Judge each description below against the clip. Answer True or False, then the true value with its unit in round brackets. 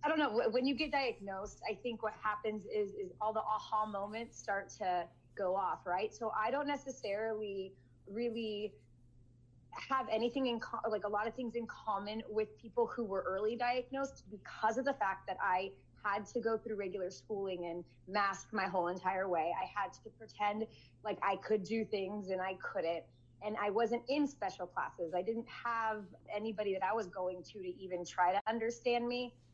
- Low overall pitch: False (210 Hz)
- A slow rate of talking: False (195 wpm)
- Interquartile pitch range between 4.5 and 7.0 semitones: False (3.5 semitones)